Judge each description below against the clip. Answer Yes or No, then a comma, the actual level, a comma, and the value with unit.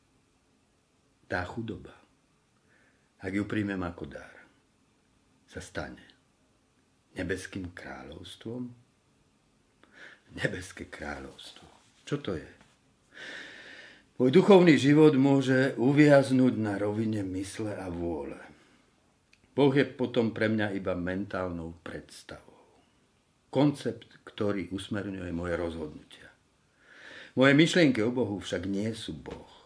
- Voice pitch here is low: Yes, low, 110 Hz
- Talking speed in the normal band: No, slow, 95 wpm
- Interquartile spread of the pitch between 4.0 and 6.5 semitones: Yes, wide, 5.6 semitones